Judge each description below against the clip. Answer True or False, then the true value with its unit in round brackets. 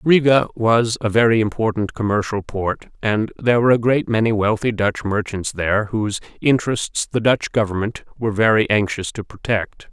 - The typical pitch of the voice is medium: False (110 Hz)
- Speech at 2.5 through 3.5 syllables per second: False (5.2 syllables/s)